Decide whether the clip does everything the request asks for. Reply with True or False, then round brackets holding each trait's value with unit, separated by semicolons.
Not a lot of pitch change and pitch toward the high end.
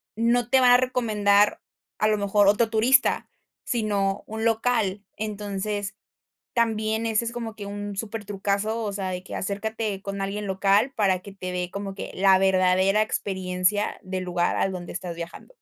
True (2.3 semitones; 205 Hz)